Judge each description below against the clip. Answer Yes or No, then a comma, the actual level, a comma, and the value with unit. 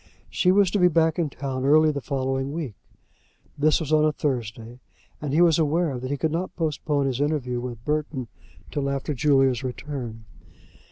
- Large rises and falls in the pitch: No, average, 3.2 semitones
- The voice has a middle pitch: Yes, medium, 145 Hz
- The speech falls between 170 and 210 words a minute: Yes, average, 185 wpm